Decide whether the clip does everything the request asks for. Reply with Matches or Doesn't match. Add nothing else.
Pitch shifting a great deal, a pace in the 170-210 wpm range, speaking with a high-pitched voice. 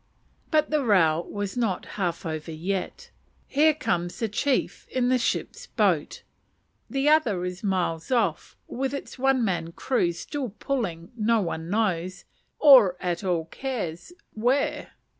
Doesn't match